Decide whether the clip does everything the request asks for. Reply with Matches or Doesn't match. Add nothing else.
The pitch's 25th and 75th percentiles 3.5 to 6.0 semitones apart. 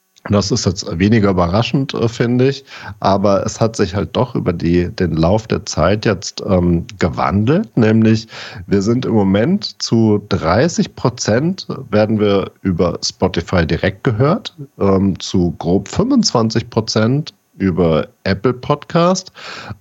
Matches